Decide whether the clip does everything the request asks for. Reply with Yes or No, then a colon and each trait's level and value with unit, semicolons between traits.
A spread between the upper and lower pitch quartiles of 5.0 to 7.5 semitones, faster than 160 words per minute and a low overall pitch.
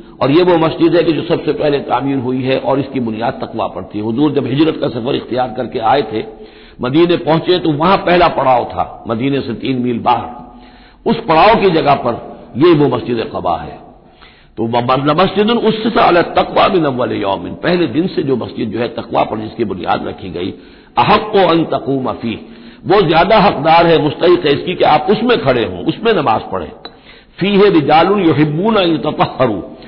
No: wide, 5.6 semitones; average, 185 wpm; medium, 150 Hz